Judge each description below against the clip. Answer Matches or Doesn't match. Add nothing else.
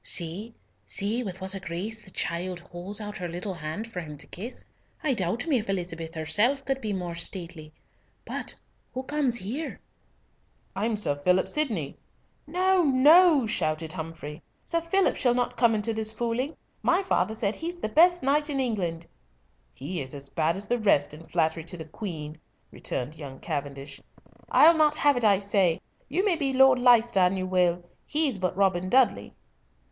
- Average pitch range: Doesn't match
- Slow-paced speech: Doesn't match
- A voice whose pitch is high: Matches